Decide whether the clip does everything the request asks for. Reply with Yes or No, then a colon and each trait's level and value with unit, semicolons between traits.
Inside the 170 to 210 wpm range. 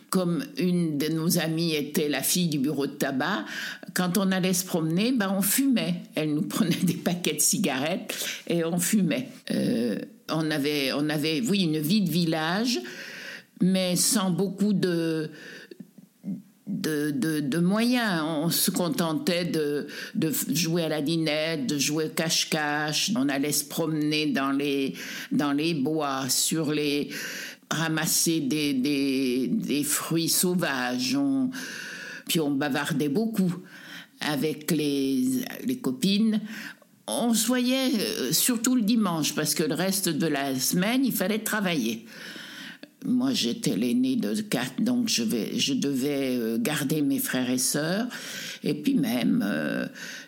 No: slow, 145 wpm